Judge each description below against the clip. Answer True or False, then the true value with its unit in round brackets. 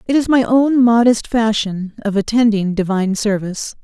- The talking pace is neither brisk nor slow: True (155 wpm)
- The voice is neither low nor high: False (220 Hz)